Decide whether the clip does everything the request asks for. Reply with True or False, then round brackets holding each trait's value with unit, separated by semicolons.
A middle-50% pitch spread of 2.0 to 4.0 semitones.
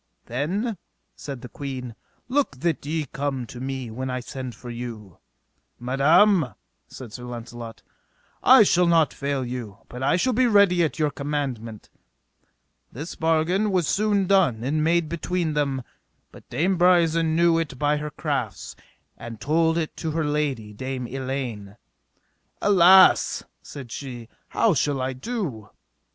False (5.2 semitones)